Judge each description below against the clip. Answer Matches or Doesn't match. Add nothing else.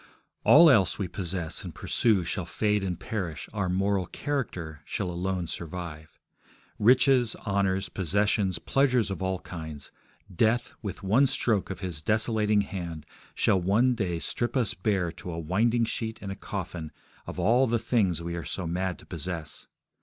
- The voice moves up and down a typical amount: Matches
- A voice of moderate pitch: Doesn't match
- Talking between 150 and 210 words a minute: Matches